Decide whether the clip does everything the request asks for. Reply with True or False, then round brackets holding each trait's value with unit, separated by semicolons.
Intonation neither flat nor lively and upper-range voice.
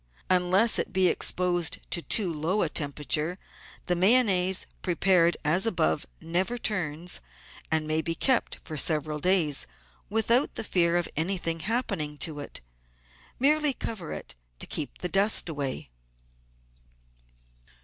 False (3.9 semitones; 175 Hz)